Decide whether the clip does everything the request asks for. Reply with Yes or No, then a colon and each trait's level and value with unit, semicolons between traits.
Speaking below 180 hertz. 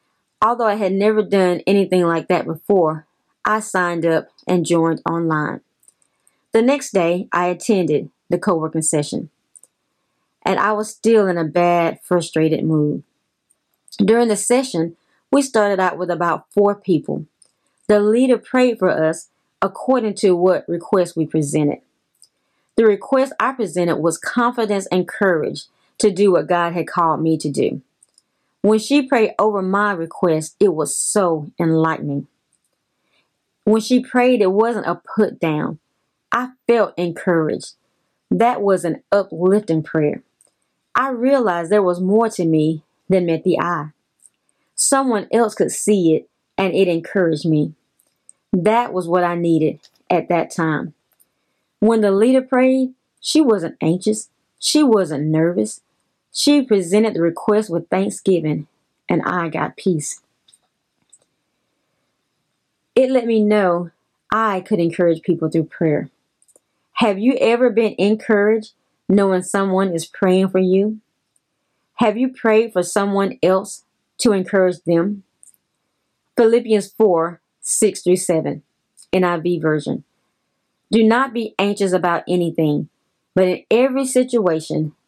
No: high, 190 Hz